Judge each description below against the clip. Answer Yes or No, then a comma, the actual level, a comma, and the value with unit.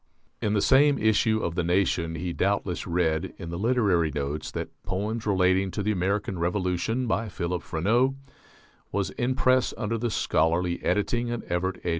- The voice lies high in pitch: No, very low, 95 Hz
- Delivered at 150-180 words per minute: Yes, average, 170 wpm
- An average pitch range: Yes, average, 4.4 semitones